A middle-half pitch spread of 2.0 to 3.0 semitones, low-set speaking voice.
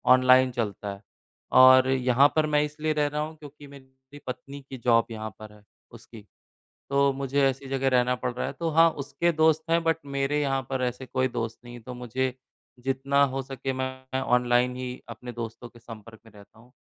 Yes: narrow, 2.5 semitones; low, 130 Hz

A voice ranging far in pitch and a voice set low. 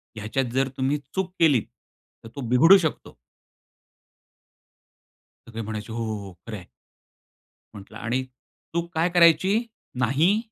Yes: wide, 6.9 semitones; low, 130 Hz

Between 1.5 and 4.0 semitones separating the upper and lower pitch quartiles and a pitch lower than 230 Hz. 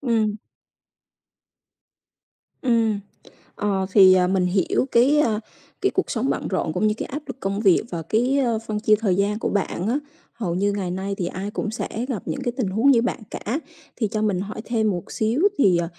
Yes: average, 3.5 semitones; high, 215 Hz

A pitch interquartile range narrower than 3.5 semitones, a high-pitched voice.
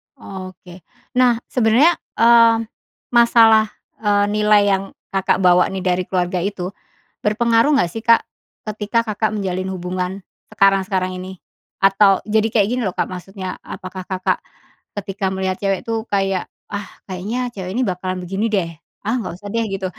Yes: average, 3.0 semitones; high, 195 Hz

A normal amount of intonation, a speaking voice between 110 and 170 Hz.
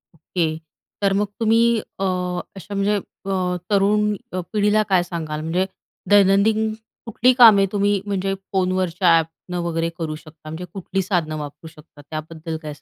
No: average, 3.7 semitones; medium, 185 Hz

